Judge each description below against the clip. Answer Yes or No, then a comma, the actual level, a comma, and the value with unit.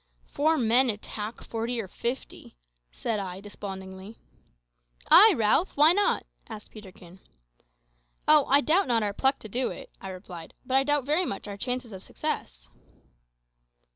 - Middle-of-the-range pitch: No, high, 225 Hz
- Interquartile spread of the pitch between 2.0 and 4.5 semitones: No, wide, 5.6 semitones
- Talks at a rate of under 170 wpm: Yes, average, 150 wpm